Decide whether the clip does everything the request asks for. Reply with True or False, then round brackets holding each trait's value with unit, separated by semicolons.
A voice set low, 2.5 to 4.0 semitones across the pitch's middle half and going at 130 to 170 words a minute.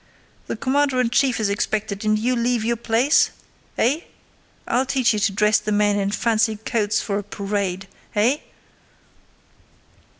False (220 Hz; 2.9 semitones; 155 wpm)